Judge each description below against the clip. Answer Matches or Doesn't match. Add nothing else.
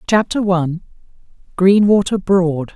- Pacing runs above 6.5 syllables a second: Doesn't match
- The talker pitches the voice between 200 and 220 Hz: Doesn't match